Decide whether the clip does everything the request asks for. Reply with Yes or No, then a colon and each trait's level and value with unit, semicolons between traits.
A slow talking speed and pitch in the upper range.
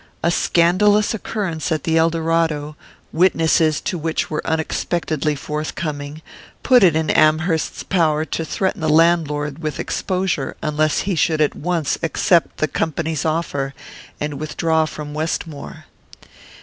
No: slow, 130 wpm; medium, 160 Hz